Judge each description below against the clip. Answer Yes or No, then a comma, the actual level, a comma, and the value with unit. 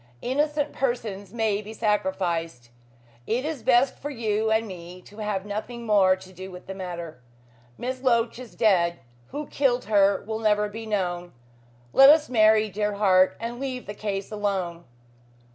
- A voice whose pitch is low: No, high, 210 Hz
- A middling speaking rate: Yes, average, 160 wpm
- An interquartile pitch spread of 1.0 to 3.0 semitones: No, average, 3.9 semitones